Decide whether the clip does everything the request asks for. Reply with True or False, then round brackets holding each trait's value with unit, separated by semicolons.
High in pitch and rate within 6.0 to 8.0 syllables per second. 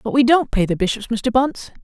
True (235 Hz; 6.1 syllables/s)